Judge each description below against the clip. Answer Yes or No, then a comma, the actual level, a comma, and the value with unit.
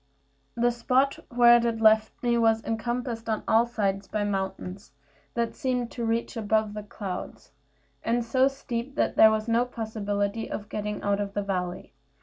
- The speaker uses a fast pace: No, average, 165 wpm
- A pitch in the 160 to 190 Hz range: No, high, 225 Hz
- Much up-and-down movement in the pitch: No, narrow, 2.5 semitones